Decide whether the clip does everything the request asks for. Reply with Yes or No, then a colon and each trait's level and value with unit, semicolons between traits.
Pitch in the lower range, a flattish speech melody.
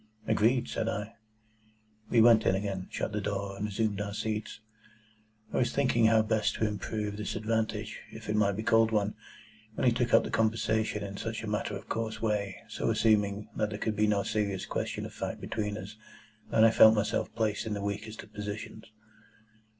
Yes: low, 105 Hz; narrow, 1.3 semitones